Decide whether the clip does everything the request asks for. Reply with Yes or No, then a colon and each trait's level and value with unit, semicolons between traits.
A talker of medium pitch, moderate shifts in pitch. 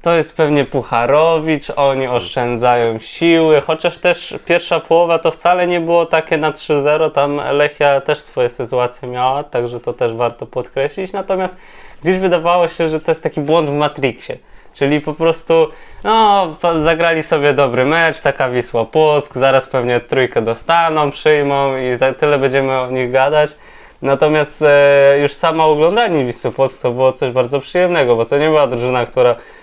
Yes: medium, 150 Hz; average, 3.9 semitones